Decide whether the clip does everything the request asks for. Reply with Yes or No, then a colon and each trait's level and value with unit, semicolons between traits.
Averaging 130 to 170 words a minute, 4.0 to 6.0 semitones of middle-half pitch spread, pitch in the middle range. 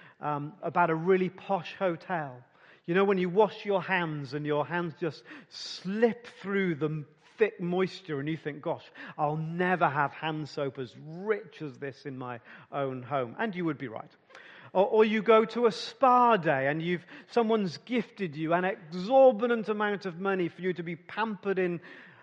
No: average, 185 wpm; average, 4.8 semitones; medium, 175 Hz